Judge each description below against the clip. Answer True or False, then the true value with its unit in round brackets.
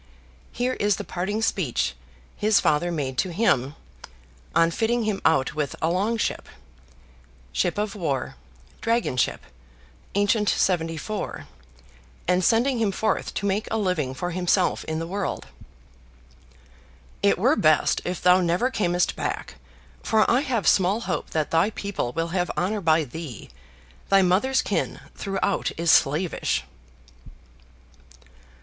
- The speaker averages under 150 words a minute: True (140 wpm)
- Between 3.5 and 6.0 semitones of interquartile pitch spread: True (4.4 semitones)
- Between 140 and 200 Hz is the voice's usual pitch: True (185 Hz)